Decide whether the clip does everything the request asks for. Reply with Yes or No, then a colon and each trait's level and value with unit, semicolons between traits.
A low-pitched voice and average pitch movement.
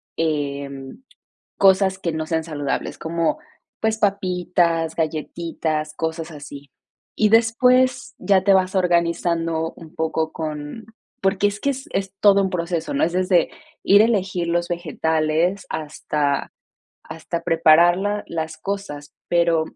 No: medium, 170 Hz; average, 3.3 semitones